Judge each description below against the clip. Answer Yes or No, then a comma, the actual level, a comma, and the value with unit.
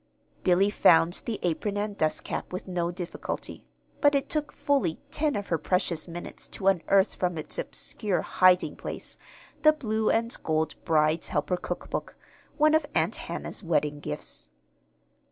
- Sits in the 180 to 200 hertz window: Yes, medium, 185 Hz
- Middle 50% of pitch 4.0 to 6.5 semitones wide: Yes, average, 4.8 semitones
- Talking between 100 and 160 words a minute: Yes, average, 155 wpm